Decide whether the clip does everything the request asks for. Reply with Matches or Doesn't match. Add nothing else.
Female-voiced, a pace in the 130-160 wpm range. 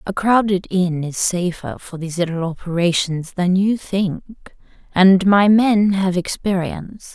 Matches